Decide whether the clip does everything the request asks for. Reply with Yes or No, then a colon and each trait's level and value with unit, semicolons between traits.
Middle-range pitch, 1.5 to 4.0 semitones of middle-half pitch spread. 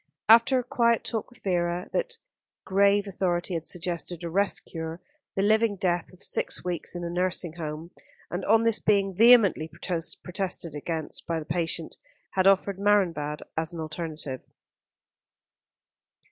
Yes: medium, 180 Hz; average, 3.5 semitones